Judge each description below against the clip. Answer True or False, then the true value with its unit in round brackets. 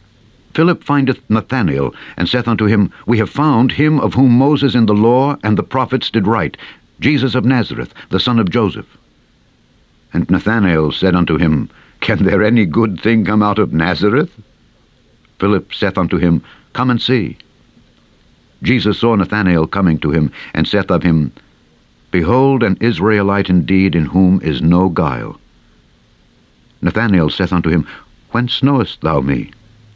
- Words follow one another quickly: False (155 wpm)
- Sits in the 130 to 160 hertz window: False (105 Hz)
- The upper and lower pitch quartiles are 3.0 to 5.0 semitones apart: False (5.4 semitones)